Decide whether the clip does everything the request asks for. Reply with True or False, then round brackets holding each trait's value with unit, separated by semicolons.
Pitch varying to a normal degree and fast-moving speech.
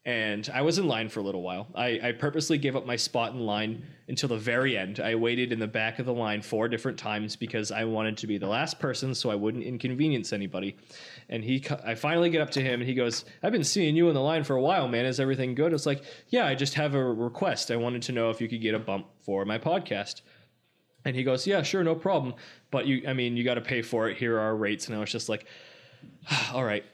True (4.0 semitones; 265 wpm)